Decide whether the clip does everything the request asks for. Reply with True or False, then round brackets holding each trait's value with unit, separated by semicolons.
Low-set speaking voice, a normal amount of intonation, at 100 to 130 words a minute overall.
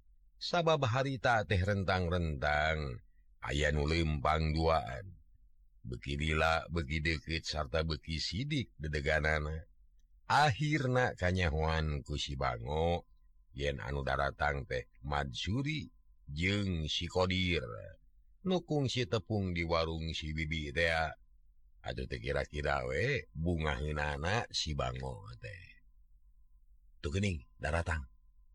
False (80 Hz; 3.4 semitones; 85 wpm)